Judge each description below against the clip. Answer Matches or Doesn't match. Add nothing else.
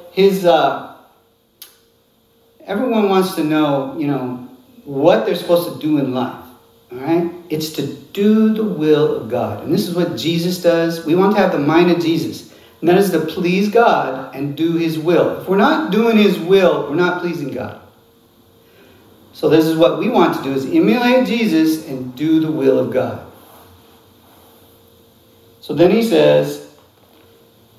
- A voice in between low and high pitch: Matches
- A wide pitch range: Matches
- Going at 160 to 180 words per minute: Matches